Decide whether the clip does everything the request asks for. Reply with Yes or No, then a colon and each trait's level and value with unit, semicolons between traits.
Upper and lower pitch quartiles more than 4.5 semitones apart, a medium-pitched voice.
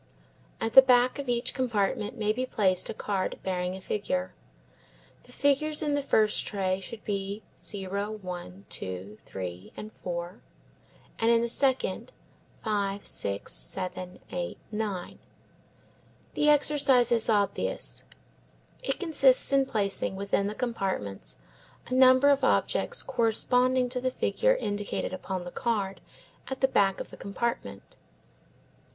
No: average, 5.2 semitones; high, 215 Hz